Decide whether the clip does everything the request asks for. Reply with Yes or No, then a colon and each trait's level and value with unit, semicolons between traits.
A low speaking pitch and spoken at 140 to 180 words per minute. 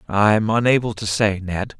Yes: low, 105 Hz; average, 165 wpm